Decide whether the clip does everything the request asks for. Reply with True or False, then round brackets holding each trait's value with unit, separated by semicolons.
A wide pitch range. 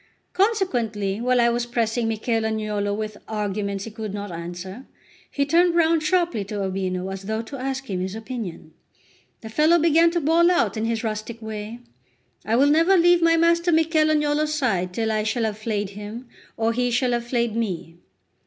True (6.4 semitones)